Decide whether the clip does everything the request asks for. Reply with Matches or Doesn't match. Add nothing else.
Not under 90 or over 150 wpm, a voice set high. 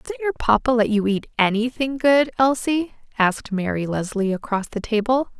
Doesn't match